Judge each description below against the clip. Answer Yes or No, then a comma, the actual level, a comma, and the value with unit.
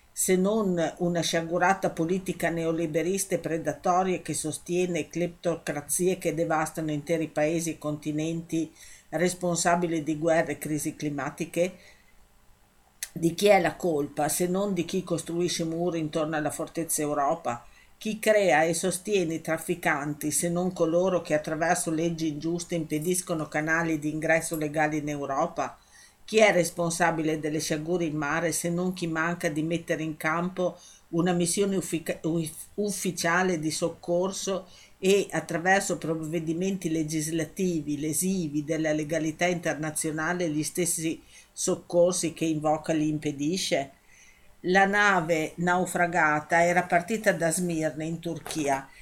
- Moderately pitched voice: Yes, medium, 165 Hz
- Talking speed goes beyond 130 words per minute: No, average, 125 wpm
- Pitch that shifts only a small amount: Yes, narrow, 2.1 semitones